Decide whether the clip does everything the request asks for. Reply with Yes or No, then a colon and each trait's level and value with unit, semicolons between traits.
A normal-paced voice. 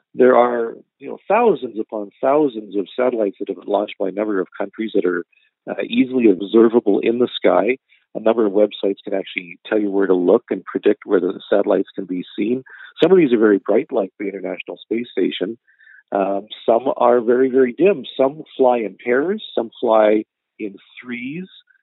Yes: average, 190 wpm